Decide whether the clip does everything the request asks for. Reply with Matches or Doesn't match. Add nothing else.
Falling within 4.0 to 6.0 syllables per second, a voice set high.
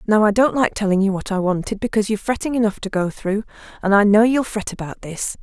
Doesn't match